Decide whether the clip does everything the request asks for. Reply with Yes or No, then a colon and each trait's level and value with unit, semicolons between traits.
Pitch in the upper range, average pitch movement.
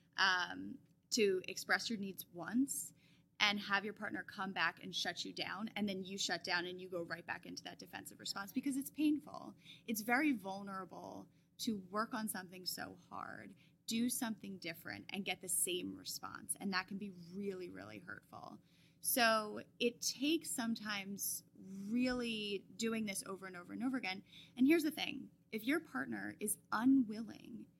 Yes: high, 200 Hz; average, 4.3 semitones